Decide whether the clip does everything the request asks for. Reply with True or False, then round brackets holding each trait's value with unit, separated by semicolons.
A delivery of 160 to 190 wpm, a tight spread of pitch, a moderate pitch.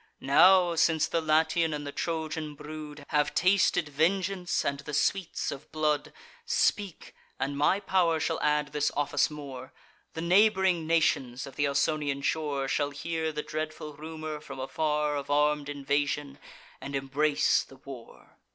False (150 wpm; 2.2 semitones; 150 Hz)